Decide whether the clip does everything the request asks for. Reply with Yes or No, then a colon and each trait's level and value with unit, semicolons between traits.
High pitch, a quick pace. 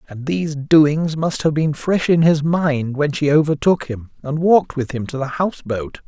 No: medium, 150 Hz; fast, 215 wpm